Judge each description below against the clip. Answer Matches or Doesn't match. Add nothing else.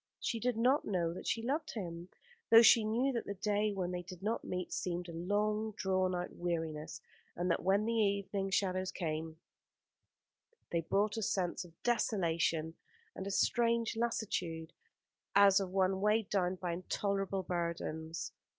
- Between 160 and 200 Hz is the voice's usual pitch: Matches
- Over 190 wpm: Doesn't match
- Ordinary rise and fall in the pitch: Matches